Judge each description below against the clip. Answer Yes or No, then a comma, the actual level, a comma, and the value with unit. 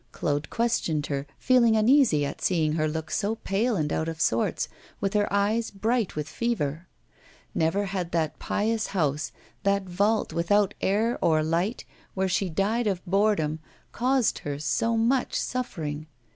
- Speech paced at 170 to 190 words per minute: No, average, 155 wpm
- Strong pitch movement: Yes, wide, 5.8 semitones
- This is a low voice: No, high, 195 Hz